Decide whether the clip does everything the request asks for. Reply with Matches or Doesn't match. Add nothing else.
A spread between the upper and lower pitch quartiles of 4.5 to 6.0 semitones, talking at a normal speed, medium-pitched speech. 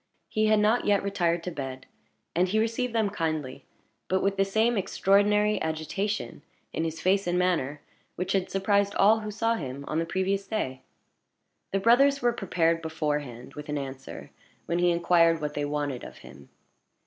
Matches